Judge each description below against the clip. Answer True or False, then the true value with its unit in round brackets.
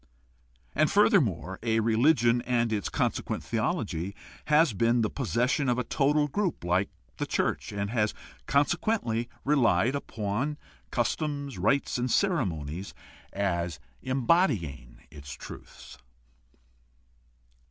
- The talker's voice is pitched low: True (120 Hz)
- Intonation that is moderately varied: False (6.1 semitones)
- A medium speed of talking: False (120 wpm)